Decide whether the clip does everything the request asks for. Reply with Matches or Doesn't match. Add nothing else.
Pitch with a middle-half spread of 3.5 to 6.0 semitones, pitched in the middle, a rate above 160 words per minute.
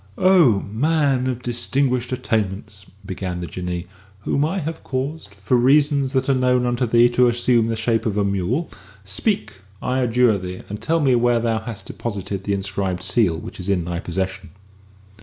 Doesn't match